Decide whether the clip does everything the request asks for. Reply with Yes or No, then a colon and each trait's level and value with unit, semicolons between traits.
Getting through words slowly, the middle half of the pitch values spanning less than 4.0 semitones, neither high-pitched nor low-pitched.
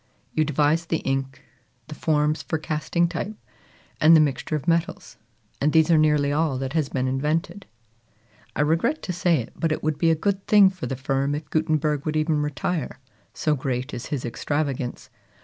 No: average, 185 wpm; average, 2.7 semitones; medium, 155 Hz